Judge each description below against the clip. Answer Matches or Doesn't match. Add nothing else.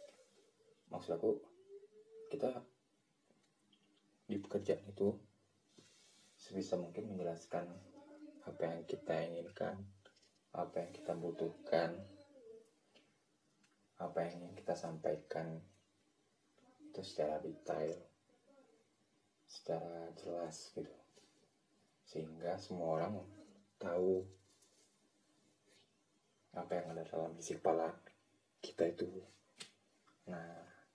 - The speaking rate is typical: Doesn't match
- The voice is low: Matches